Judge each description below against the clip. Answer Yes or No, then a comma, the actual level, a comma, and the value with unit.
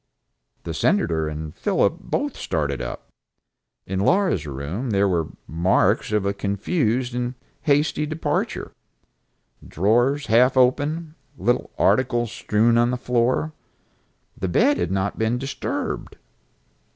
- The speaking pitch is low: Yes, low, 120 Hz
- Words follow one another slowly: Yes, slow, 125 wpm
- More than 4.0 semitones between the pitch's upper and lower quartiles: Yes, wide, 5.4 semitones